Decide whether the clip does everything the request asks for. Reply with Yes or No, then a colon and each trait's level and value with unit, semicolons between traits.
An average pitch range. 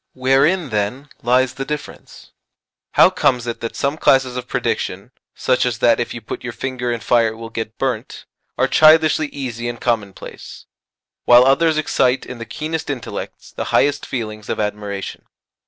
Yes: average, 3.0 semitones